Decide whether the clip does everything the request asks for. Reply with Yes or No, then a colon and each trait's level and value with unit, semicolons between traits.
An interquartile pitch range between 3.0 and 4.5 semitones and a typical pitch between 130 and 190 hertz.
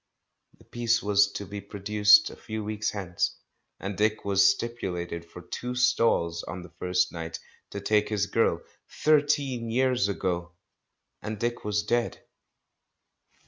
No: average, 3.7 semitones; low, 105 Hz